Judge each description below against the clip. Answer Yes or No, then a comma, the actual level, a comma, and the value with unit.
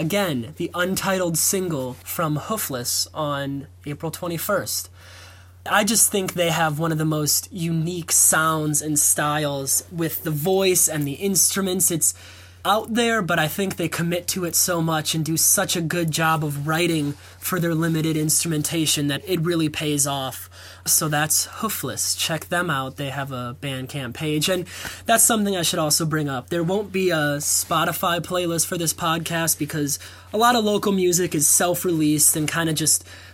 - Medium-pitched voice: Yes, medium, 160 Hz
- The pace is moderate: Yes, average, 175 wpm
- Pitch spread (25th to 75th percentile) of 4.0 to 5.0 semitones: No, average, 3.6 semitones